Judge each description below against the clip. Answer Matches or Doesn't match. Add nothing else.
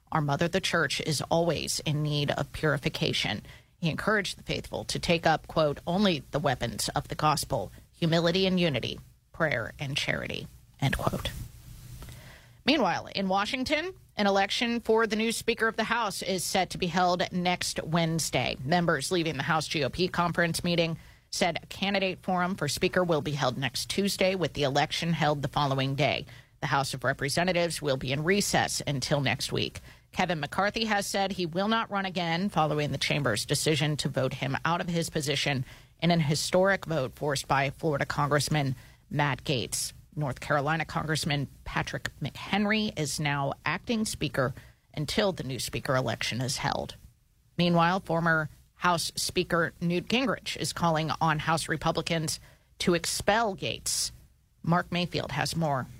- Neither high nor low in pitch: Matches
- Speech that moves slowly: Doesn't match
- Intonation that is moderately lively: Matches